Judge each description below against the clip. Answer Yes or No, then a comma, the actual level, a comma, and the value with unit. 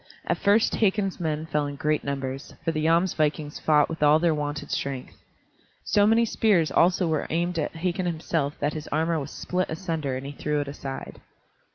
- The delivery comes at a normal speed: Yes, average, 190 wpm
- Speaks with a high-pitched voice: No, medium, 155 Hz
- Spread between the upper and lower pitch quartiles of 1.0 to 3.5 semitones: Yes, average, 2.9 semitones